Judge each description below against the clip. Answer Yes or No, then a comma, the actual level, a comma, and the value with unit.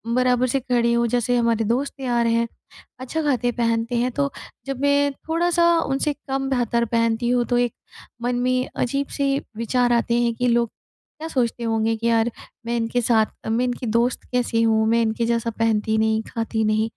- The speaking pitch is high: Yes, high, 240 Hz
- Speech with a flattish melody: Yes, narrow, 1.8 semitones